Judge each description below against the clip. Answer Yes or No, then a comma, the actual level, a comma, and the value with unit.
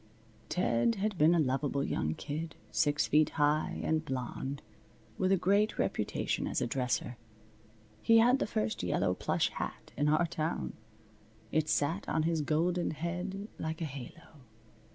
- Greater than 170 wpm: No, average, 155 wpm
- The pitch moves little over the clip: No, average, 3.6 semitones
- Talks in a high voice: No, medium, 155 Hz